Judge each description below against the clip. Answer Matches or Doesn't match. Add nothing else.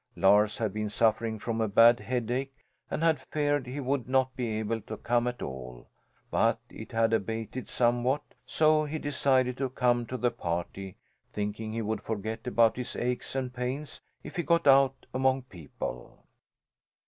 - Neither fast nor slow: Matches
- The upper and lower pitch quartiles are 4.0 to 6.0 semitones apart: Doesn't match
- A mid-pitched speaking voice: Doesn't match